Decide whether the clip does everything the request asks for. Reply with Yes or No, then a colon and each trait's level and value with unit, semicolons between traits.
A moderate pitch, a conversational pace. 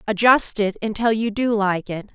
No: high, 215 Hz; average, 195 wpm